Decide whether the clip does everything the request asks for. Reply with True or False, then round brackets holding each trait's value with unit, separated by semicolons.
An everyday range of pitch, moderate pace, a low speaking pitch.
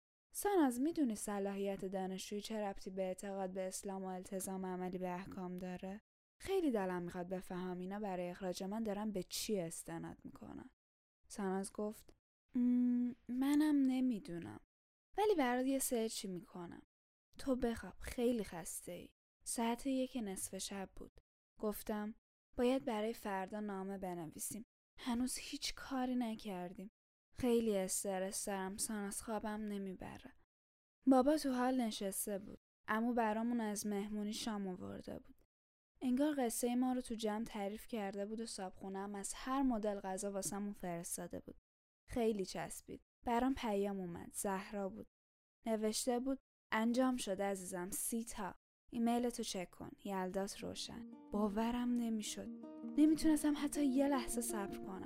False (4.3 semitones; 135 wpm; 215 Hz)